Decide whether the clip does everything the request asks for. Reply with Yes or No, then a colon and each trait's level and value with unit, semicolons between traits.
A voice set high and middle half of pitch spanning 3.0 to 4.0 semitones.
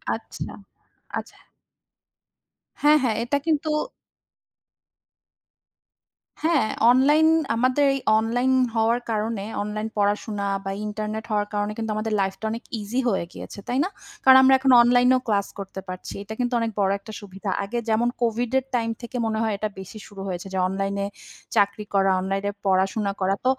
Yes: high, 220 Hz; average, 3.5 semitones